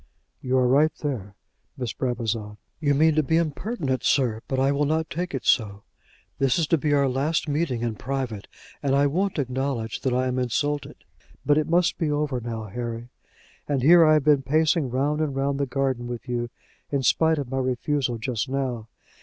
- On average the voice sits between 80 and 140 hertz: Yes, low, 135 Hz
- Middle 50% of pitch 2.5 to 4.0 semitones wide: Yes, average, 3.4 semitones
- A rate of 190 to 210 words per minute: Yes, average, 195 wpm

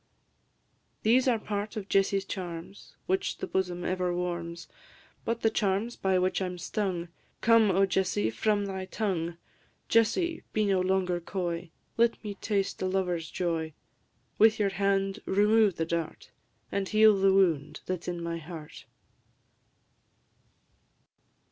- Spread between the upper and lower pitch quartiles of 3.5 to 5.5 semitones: No, average, 2.9 semitones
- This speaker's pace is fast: No, average, 140 wpm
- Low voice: No, high, 190 Hz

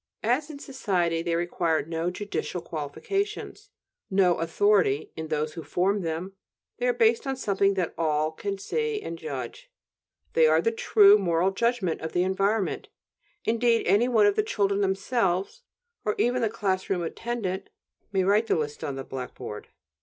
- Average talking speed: Yes, average, 165 wpm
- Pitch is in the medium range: No, high, 195 Hz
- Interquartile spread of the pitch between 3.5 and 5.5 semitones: Yes, average, 5.2 semitones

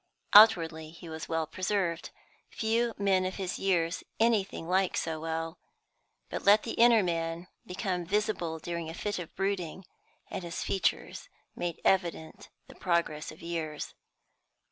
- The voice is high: No, medium, 175 Hz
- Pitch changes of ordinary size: Yes, average, 3.1 semitones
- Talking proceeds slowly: No, average, 145 wpm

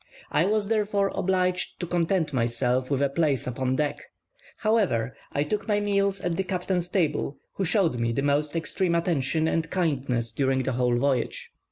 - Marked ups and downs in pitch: Yes, wide, 6.0 semitones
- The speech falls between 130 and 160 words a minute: No, average, 175 wpm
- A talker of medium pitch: Yes, medium, 160 Hz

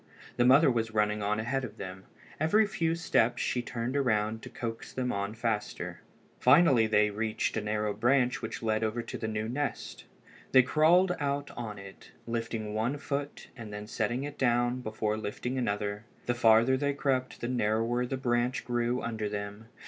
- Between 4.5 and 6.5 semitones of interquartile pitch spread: No, average, 3.2 semitones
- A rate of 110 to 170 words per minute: No, average, 180 wpm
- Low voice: Yes, low, 120 Hz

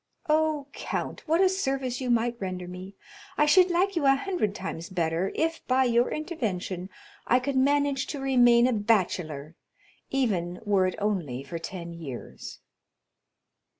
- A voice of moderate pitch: No, high, 235 Hz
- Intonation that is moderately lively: No, wide, 7.6 semitones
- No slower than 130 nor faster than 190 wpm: Yes, average, 150 wpm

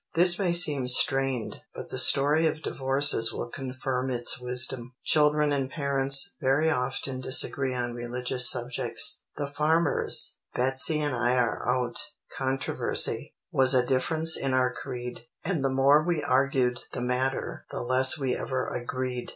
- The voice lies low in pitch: Yes, low, 130 Hz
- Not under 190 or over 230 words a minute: No, average, 150 wpm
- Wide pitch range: No, narrow, 2.5 semitones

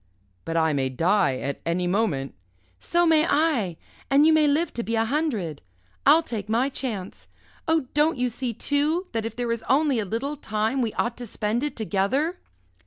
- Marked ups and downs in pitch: Yes, wide, 6.6 semitones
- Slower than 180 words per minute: No, average, 190 wpm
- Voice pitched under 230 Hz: No, high, 235 Hz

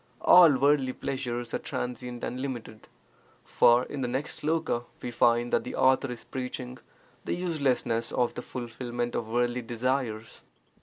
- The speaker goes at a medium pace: Yes, average, 150 wpm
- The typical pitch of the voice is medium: No, low, 125 Hz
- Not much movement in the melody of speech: Yes, narrow, 1.9 semitones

